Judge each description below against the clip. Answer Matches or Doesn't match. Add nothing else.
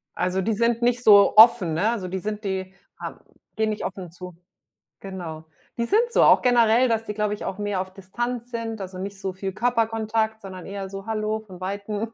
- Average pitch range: Matches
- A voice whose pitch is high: Matches